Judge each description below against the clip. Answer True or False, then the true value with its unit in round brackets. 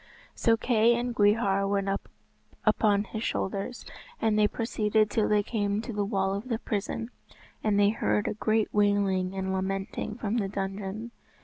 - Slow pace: False (165 wpm)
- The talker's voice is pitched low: False (205 Hz)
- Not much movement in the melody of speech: True (2.0 semitones)